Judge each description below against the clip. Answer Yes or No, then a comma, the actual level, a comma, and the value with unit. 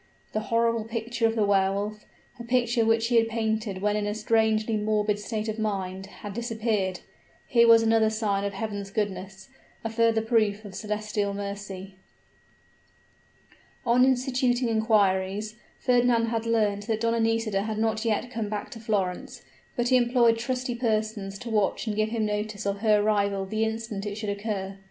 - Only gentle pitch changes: Yes, narrow, 2.1 semitones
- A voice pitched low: No, high, 215 Hz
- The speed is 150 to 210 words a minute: Yes, average, 170 wpm